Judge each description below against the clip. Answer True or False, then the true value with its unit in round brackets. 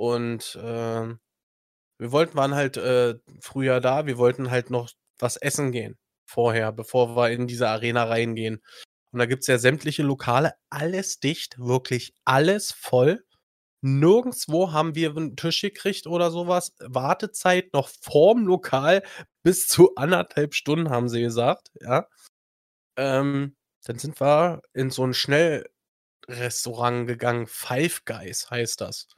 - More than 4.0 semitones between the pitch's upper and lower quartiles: True (4.4 semitones)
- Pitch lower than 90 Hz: False (130 Hz)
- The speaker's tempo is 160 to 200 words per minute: False (140 wpm)